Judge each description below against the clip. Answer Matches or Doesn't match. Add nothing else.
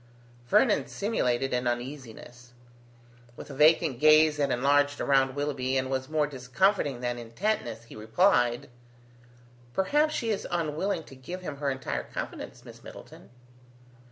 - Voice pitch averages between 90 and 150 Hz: Matches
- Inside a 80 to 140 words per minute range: Matches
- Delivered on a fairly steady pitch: Doesn't match